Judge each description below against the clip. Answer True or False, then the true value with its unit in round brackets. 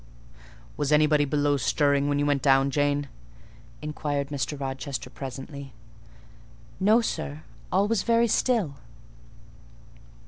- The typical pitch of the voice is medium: True (145 Hz)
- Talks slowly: True (110 wpm)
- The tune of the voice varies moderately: False (2.0 semitones)